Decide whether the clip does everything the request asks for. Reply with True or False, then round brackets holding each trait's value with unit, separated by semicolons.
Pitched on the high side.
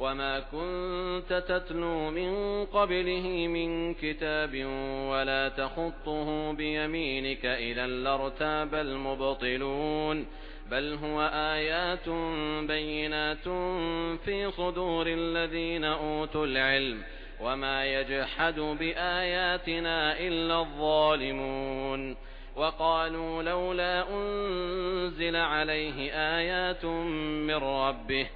False (155 Hz)